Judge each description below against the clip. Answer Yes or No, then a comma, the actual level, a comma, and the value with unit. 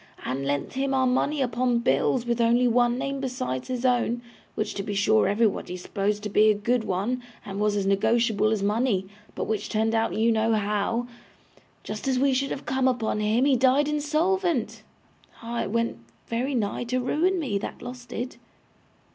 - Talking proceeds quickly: No, average, 190 wpm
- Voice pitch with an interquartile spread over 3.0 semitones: Yes, average, 3.4 semitones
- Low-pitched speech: No, high, 235 Hz